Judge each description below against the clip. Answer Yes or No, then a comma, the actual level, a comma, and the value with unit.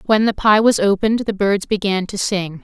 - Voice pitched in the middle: No, high, 205 Hz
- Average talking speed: No, fast, 230 wpm